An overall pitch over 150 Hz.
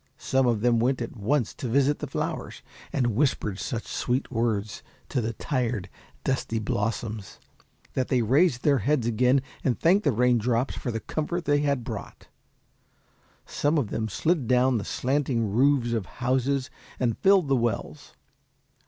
No: low, 125 Hz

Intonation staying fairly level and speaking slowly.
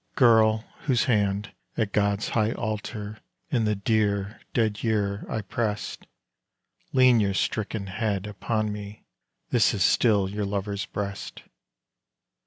Yes: narrow, 1.6 semitones; slow, 125 wpm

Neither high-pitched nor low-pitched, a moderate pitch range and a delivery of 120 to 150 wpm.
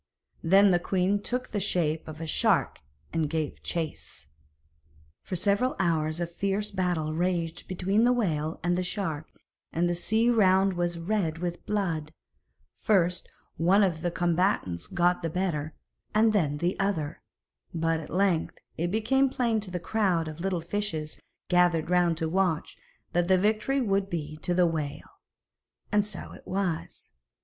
No: medium, 180 Hz; average, 3.4 semitones; average, 160 wpm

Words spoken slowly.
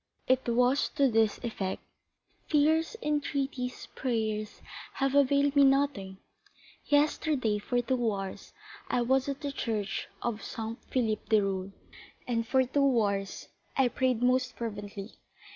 Yes: slow, 130 wpm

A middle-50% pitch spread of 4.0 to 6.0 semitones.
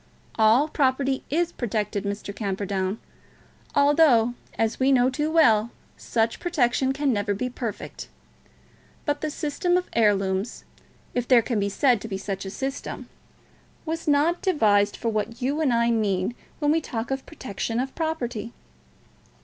Yes: wide, 5.5 semitones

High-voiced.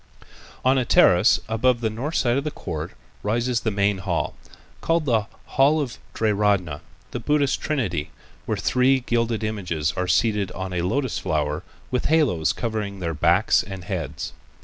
No: low, 110 Hz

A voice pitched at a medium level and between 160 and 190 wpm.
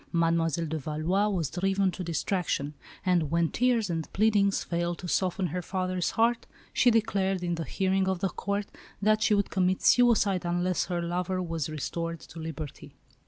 Yes: medium, 180 Hz; average, 170 wpm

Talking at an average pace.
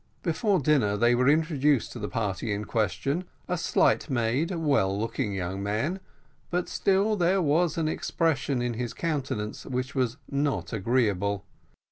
Yes: average, 150 wpm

